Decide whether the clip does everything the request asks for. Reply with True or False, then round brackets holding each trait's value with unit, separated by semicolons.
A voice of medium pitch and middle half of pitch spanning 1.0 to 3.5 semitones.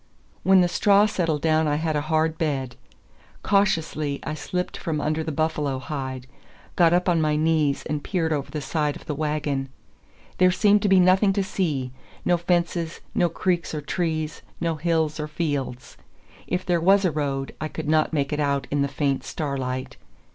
True (155 Hz; 3.1 semitones)